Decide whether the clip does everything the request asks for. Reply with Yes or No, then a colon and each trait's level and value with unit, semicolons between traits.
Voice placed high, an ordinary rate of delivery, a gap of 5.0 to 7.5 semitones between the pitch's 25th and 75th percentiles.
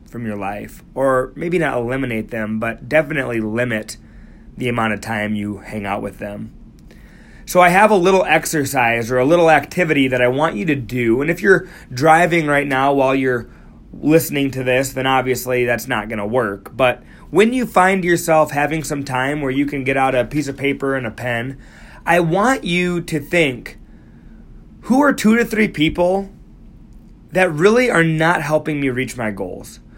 No: low, 135 Hz; average, 190 wpm; wide, 5.5 semitones